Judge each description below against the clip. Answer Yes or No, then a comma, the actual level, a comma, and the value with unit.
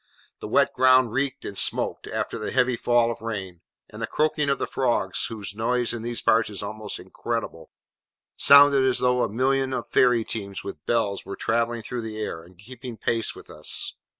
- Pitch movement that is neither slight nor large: Yes, average, 3.5 semitones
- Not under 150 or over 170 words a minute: No, average, 195 wpm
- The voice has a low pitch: Yes, low, 115 Hz